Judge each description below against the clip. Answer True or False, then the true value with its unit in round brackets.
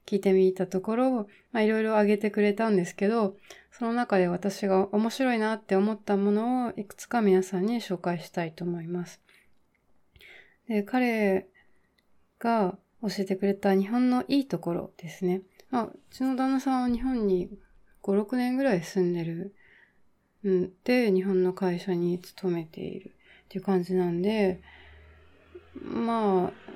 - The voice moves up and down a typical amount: True (3.3 semitones)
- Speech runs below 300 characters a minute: True (285 characters per minute)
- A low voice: False (200 Hz)